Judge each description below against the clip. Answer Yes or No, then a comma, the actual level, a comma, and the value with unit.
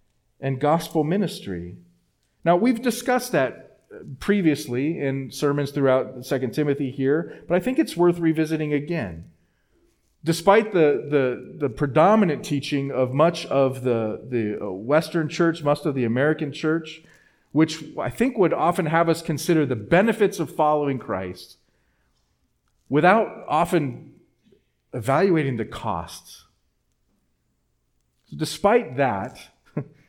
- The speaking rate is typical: No, slow, 120 wpm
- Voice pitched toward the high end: No, medium, 150 Hz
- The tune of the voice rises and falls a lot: No, average, 4.6 semitones